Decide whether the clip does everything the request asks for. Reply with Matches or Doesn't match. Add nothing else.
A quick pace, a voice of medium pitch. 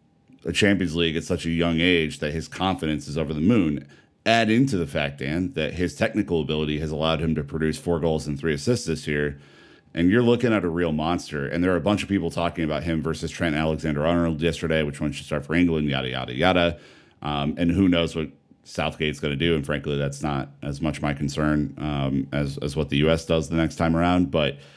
Doesn't match